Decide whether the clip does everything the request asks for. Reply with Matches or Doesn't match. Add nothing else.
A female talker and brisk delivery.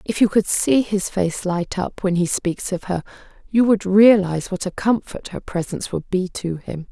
Matches